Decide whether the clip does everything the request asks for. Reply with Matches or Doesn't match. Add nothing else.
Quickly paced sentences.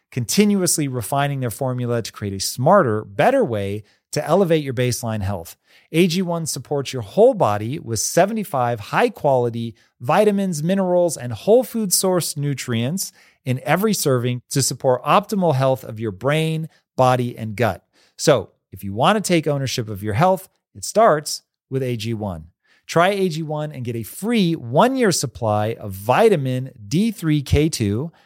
Doesn't match